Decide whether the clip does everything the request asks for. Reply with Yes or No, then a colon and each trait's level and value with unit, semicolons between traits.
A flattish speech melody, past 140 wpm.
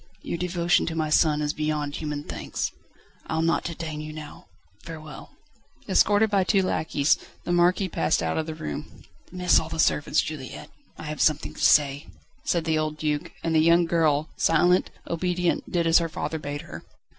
Yes: narrow, 2.1 semitones; average, 180 wpm